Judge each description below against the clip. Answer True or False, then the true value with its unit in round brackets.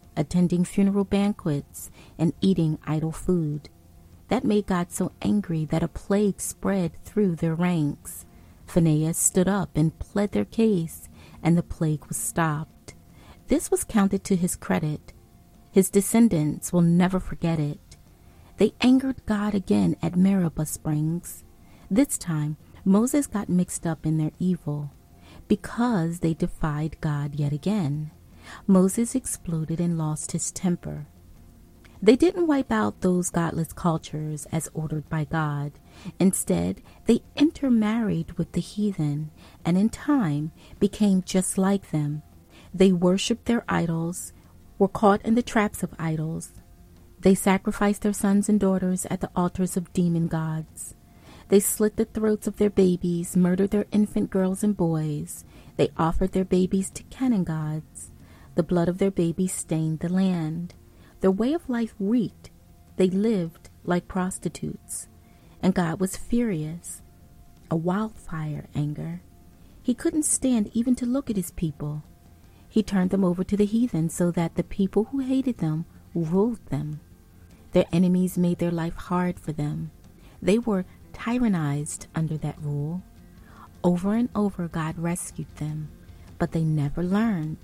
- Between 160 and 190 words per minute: False (145 wpm)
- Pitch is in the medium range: True (175 Hz)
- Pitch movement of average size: True (4.7 semitones)